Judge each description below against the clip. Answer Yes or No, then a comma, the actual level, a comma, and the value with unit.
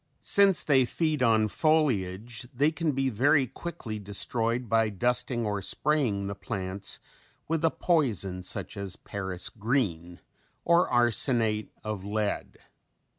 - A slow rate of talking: Yes, slow, 125 wpm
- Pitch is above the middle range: No, low, 115 Hz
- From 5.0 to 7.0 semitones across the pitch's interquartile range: Yes, wide, 5.6 semitones